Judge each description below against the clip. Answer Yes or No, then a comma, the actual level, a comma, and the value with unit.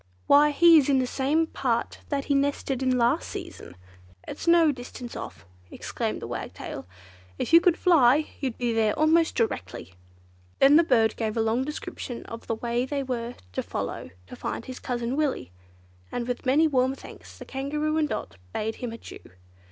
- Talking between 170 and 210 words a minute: Yes, average, 185 wpm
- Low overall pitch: No, very high, 260 Hz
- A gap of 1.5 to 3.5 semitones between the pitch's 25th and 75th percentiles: No, average, 4.1 semitones